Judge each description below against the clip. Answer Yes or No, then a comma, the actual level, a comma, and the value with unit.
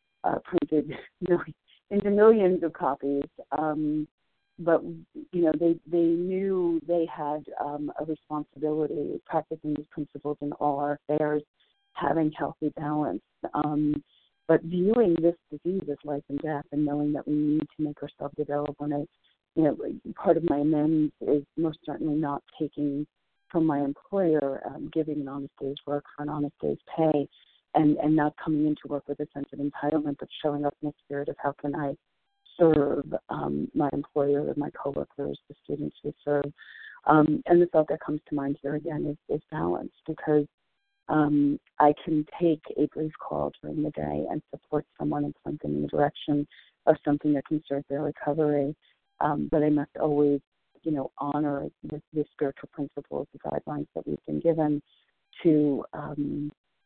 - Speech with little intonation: Yes, narrow, 1.5 semitones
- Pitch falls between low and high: Yes, medium, 150 Hz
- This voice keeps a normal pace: Yes, average, 170 wpm